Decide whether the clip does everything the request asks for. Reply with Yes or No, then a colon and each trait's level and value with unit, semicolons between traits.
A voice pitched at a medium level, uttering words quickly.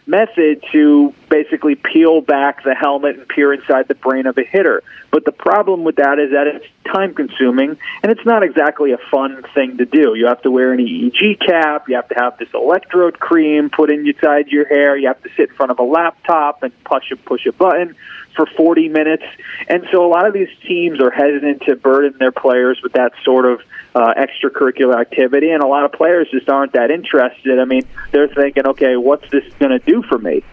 Yes: medium, 145 Hz; fast, 220 wpm